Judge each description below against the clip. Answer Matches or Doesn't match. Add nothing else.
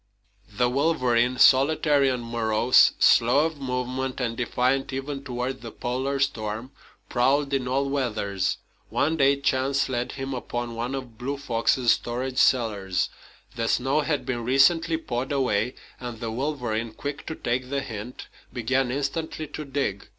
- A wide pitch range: Doesn't match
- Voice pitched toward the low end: Matches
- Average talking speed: Matches